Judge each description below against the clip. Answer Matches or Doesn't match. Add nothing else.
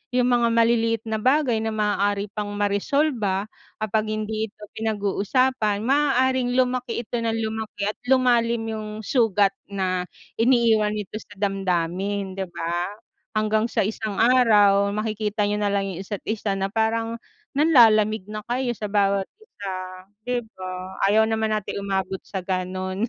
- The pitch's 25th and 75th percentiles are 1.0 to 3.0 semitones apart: Matches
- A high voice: Matches